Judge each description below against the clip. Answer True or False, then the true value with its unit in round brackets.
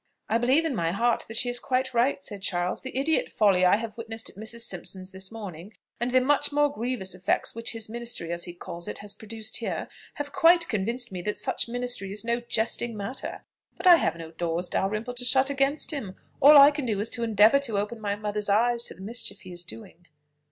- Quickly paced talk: True (230 wpm)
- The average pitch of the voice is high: True (225 Hz)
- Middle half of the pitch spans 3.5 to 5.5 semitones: True (4.0 semitones)